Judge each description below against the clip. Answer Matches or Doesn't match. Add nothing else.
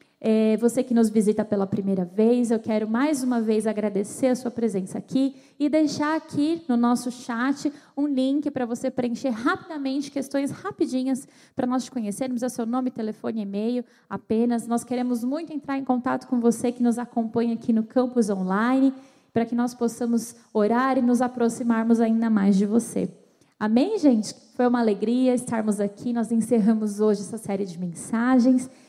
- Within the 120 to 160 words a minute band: Doesn't match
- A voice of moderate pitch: Doesn't match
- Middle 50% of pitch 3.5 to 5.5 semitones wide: Doesn't match